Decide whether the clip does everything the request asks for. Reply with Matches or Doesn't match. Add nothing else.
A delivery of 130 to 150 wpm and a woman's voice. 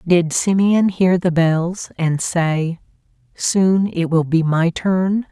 Matches